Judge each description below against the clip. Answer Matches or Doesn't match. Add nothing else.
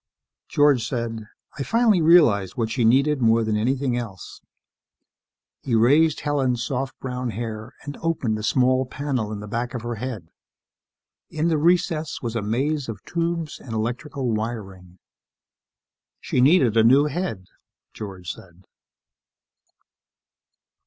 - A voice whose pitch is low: Matches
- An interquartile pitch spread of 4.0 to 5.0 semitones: Matches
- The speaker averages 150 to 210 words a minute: Doesn't match